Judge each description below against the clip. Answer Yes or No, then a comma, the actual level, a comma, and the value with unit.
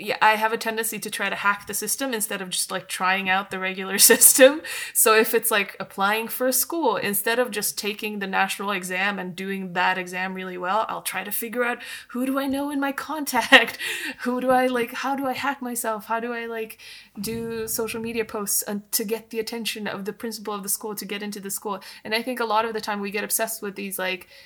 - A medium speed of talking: No, fast, 245 wpm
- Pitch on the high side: Yes, high, 220 Hz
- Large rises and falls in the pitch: No, narrow, 2.6 semitones